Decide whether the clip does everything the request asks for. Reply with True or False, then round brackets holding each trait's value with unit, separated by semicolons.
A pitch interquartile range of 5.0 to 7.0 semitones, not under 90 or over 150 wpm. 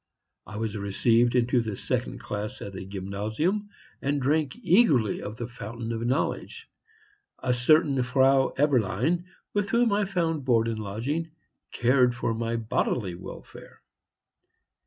True (5.5 semitones; 135 wpm)